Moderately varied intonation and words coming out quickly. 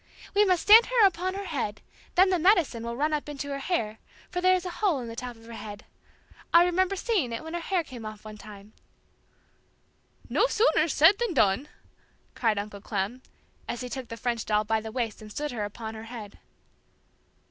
No: wide, 8.4 semitones; fast, 210 wpm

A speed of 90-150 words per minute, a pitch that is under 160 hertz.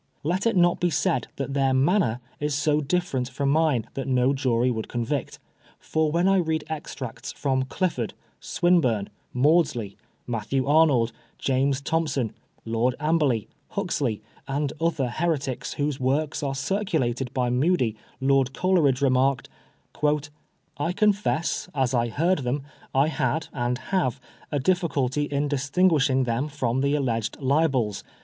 Yes: average, 140 wpm; medium, 140 Hz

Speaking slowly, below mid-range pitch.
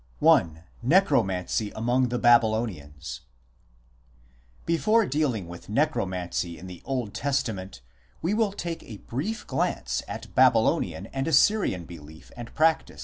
Yes: slow, 120 wpm; low, 120 Hz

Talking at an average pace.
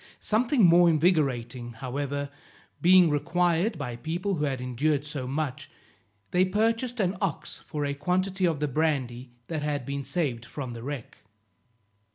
Yes: average, 150 wpm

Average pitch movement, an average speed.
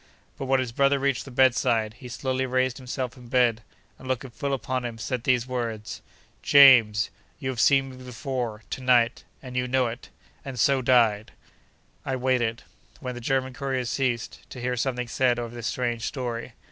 No: narrow, 1.8 semitones; average, 185 wpm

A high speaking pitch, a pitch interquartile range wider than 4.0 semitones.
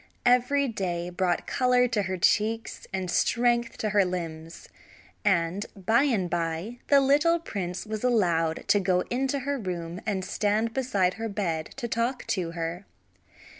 Yes: high, 205 Hz; average, 5.3 semitones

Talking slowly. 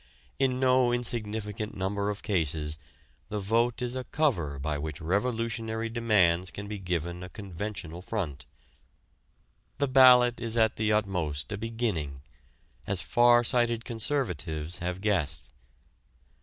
Yes: slow, 130 wpm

